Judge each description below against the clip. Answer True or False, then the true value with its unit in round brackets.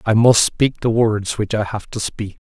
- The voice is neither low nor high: False (110 Hz)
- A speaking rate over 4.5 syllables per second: False (4.4 syllables/s)